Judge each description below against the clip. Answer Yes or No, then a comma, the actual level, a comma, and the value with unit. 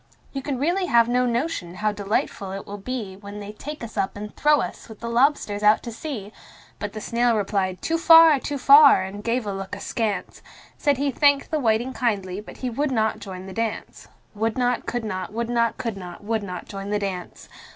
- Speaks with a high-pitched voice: Yes, high, 225 Hz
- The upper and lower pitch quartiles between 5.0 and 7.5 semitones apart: No, average, 4.0 semitones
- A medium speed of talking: No, fast, 215 wpm